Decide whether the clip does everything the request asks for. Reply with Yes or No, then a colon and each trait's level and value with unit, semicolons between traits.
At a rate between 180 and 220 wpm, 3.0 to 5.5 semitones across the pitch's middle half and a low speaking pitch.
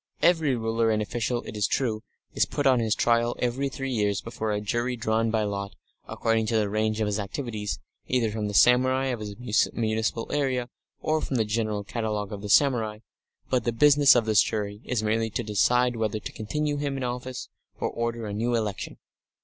No: average, 200 wpm; narrow, 2.6 semitones; low, 115 Hz